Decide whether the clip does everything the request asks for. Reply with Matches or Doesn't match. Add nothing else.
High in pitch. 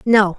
Matches